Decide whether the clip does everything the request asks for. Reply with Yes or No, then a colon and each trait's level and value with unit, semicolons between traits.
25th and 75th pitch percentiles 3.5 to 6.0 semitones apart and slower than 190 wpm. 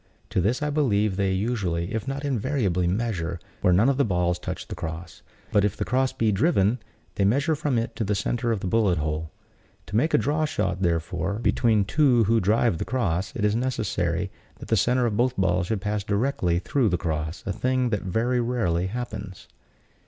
No: average, 5.2 semitones; fast, 205 wpm